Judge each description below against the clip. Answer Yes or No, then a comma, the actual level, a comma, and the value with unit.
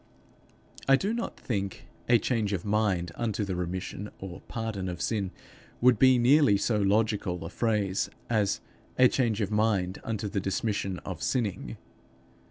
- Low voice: Yes, low, 105 Hz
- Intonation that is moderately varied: Yes, average, 3.1 semitones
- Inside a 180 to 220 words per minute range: No, average, 155 wpm